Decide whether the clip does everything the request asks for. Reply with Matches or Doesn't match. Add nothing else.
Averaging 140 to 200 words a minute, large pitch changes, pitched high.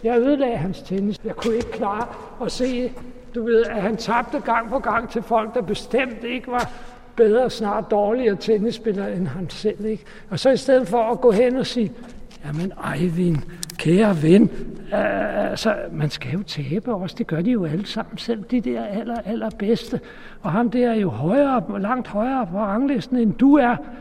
Doesn't match